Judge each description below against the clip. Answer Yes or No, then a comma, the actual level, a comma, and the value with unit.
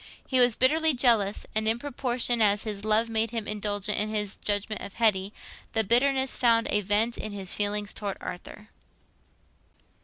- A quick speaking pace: No, average, 165 wpm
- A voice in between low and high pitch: No, high, 215 Hz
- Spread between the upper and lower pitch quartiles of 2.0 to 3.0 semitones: Yes, narrow, 2.6 semitones